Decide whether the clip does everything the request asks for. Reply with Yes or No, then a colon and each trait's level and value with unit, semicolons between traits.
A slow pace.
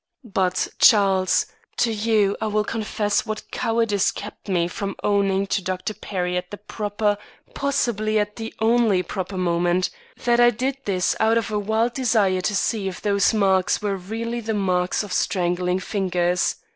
No: average, 165 wpm